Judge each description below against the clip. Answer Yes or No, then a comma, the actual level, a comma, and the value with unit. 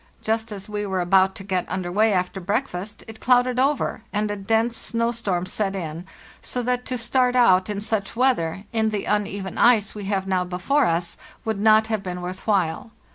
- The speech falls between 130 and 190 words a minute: No, average, 200 wpm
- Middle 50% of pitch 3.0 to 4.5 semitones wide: Yes, average, 3.4 semitones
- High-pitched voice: Yes, high, 205 Hz